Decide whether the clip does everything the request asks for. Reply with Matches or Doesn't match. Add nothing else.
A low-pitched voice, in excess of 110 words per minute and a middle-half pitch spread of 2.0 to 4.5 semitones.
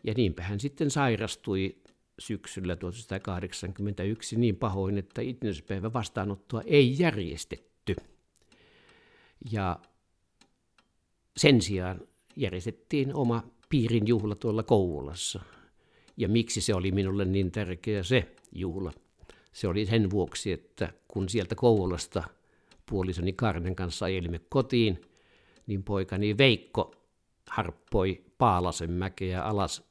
Doesn't match